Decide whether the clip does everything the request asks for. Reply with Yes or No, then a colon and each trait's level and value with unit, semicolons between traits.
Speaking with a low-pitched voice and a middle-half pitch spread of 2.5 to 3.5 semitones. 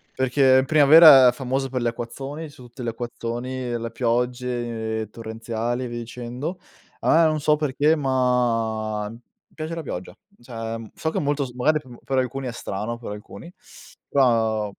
Yes: low, 125 Hz; average, 2.8 semitones